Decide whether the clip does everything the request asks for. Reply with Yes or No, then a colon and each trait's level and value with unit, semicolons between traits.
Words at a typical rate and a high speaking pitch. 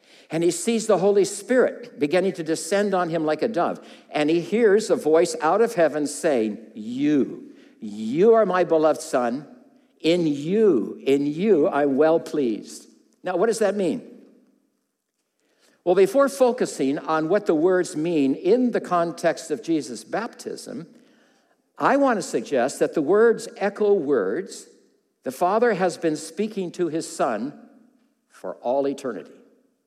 Yes: average, 150 wpm; high, 200 Hz